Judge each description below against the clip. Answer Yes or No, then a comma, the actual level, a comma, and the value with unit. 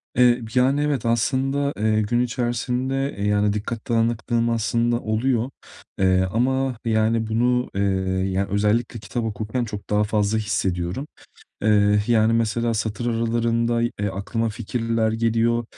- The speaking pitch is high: No, low, 115 Hz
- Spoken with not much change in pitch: Yes, narrow, 2.1 semitones